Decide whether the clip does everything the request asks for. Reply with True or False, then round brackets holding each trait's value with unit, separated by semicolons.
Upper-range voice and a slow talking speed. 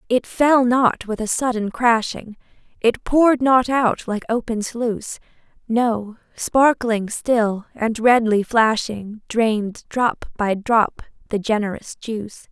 True (230 Hz; 130 wpm)